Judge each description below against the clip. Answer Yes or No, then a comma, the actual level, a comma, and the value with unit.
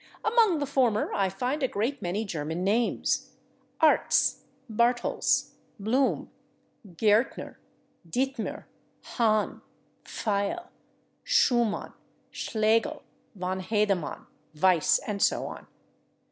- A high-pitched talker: Yes, high, 220 Hz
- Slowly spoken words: Yes, slow, 90 wpm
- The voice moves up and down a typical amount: Yes, average, 4.5 semitones